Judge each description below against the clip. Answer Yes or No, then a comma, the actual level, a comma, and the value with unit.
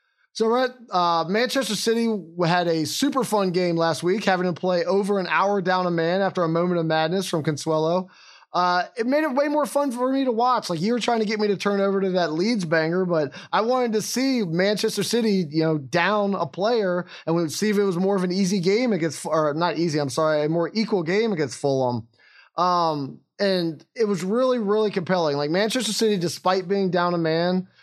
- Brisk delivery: Yes, fast, 225 wpm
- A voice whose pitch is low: No, medium, 185 Hz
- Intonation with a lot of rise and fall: No, average, 4.3 semitones